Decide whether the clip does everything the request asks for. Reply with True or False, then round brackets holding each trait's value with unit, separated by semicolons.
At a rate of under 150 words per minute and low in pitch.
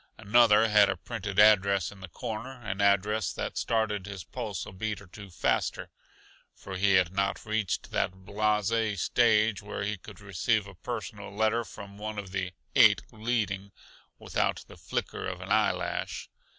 False (175 wpm; 105 Hz)